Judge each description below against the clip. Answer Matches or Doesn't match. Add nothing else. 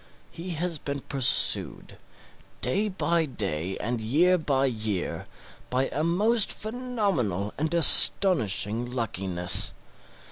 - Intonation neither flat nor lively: Doesn't match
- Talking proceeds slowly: Matches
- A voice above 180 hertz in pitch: Doesn't match